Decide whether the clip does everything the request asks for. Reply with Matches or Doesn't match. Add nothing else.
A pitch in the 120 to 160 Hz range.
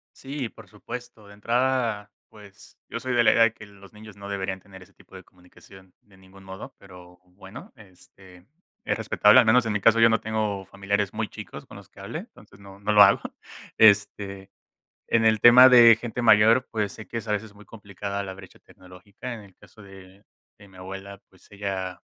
Doesn't match